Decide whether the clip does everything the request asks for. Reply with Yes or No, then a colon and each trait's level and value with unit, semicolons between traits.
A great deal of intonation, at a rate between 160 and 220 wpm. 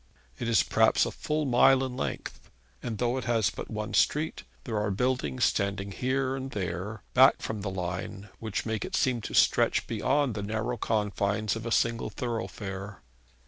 No: average, 3.8 semitones; average, 180 wpm